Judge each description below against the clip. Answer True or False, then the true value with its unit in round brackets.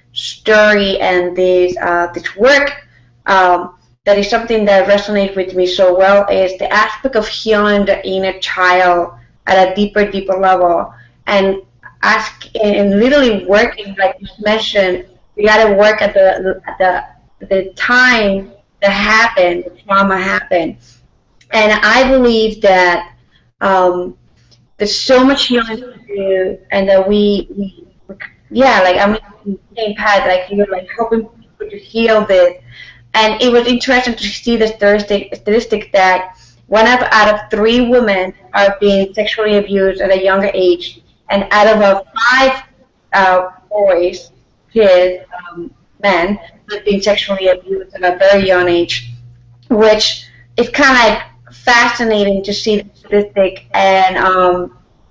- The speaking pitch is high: True (200 Hz)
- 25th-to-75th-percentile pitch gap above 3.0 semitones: False (2.7 semitones)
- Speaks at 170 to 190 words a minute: False (145 wpm)